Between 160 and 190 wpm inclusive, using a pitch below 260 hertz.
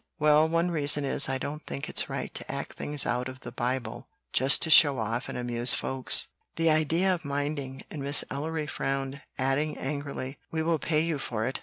No: average, 200 wpm; medium, 140 Hz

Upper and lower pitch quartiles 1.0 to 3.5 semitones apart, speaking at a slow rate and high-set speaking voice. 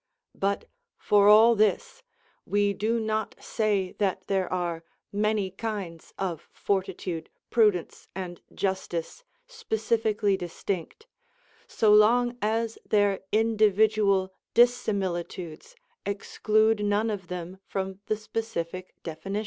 Yes: narrow, 2.6 semitones; slow, 105 wpm; high, 205 Hz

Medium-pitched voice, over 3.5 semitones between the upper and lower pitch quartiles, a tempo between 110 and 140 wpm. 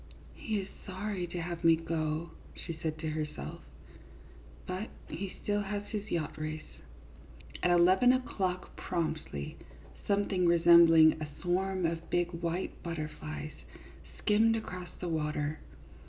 No: medium, 170 Hz; average, 3.1 semitones; slow, 135 wpm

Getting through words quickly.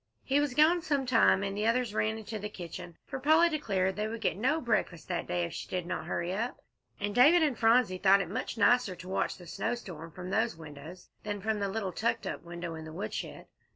Yes: fast, 230 wpm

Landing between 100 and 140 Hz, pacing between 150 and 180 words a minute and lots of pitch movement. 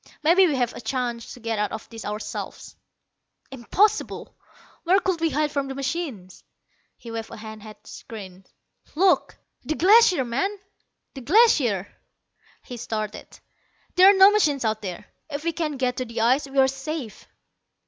No: very high, 265 Hz; average, 170 wpm; wide, 6.8 semitones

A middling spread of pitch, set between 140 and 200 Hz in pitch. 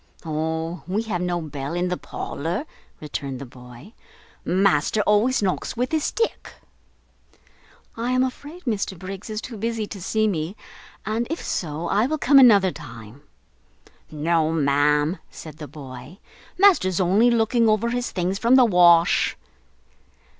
No: wide, 6.6 semitones; medium, 185 Hz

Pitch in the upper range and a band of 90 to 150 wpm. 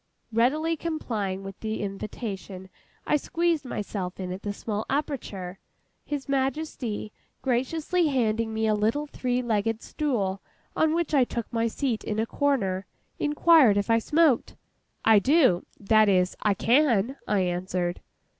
Yes: high, 225 Hz; average, 140 wpm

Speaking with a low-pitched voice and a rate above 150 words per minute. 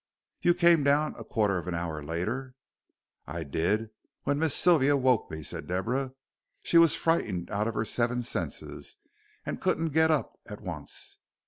Yes: low, 120 Hz; average, 165 wpm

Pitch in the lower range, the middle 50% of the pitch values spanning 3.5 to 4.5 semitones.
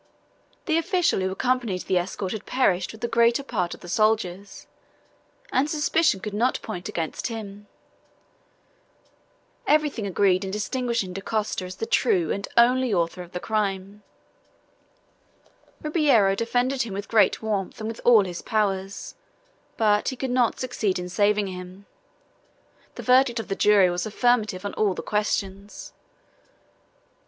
No: high, 210 Hz; average, 4.0 semitones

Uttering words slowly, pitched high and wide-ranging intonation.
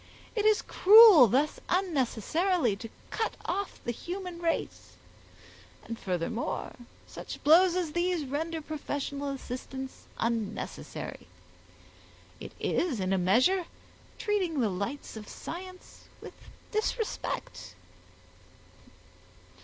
Yes: slow, 100 wpm; very high, 310 Hz; wide, 7.4 semitones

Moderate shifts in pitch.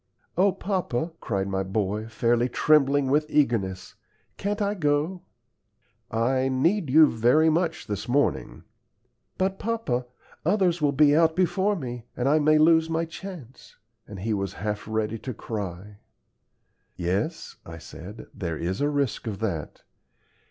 No: wide, 7.3 semitones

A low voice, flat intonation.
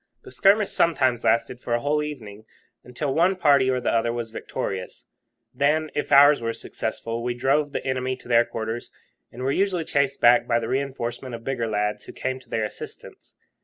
No: low, 130 Hz; average, 3.5 semitones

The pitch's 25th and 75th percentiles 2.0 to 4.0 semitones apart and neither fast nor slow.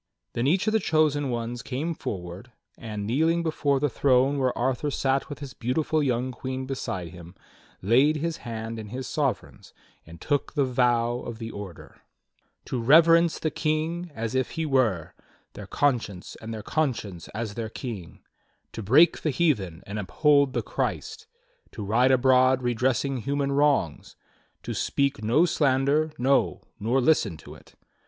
No: average, 4.4 semitones; average, 160 wpm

